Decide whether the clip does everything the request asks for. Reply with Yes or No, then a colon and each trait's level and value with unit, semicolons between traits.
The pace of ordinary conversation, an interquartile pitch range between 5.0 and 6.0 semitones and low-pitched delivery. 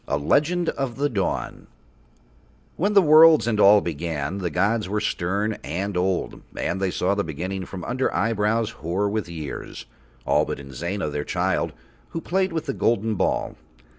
Yes: average, 165 wpm; wide, 5.6 semitones; low, 100 Hz